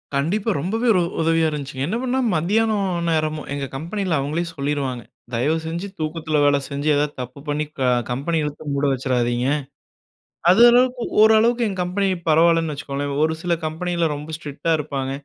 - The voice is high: No, medium, 160 Hz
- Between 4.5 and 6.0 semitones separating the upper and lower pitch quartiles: No, average, 4.1 semitones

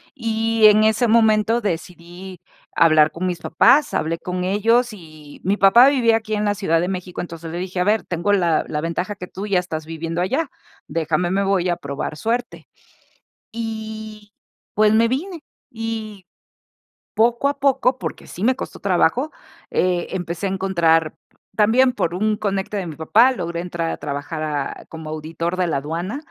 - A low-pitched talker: No, high, 190 Hz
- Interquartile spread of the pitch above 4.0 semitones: Yes, average, 4.8 semitones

